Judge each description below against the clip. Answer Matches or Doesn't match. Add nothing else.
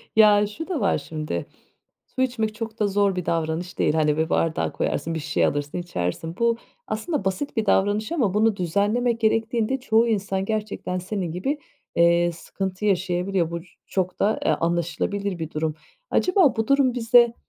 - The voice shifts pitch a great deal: Doesn't match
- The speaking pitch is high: Matches